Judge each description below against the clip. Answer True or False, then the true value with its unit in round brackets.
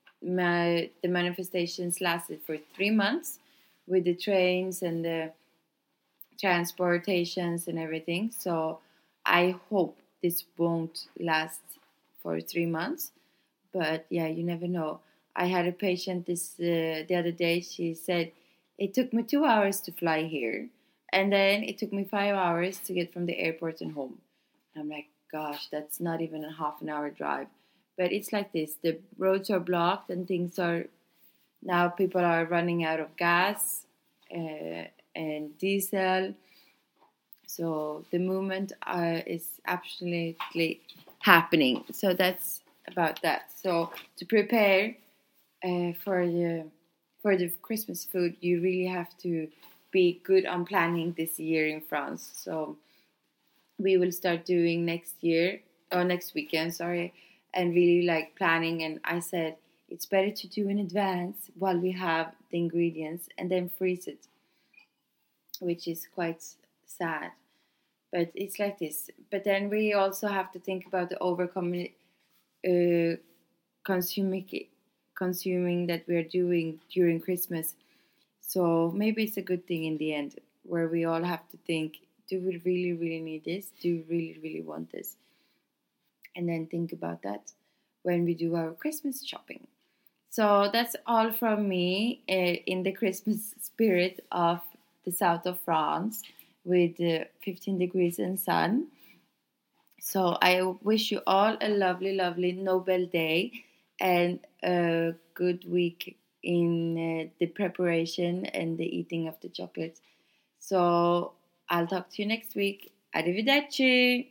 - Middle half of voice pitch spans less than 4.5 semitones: True (2.4 semitones)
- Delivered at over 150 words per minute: False (145 wpm)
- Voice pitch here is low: False (175 Hz)